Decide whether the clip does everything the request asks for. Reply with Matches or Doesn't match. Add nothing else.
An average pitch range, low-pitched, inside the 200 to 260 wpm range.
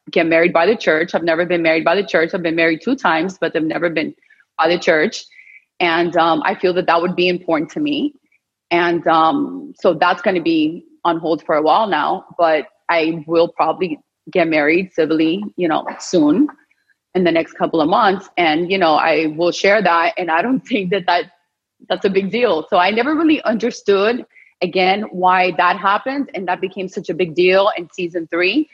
Doesn't match